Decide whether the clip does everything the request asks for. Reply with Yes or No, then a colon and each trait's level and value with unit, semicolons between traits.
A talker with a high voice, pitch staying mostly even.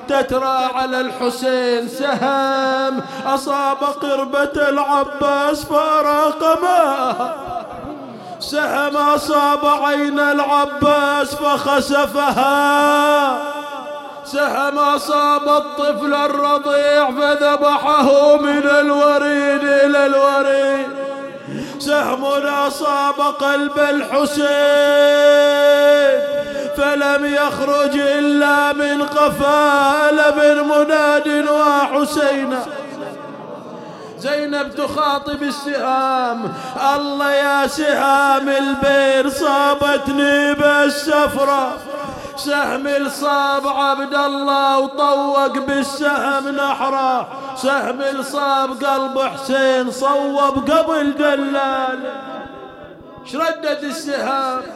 Yes: very high, 285 Hz; narrow, 0.8 semitones